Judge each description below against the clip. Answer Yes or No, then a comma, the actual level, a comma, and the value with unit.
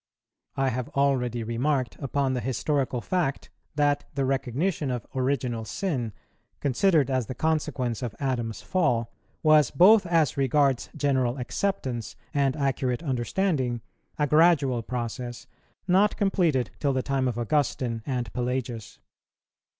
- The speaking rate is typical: No, slow, 130 wpm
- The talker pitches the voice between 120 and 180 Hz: Yes, low, 135 Hz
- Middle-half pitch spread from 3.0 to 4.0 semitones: Yes, average, 3.4 semitones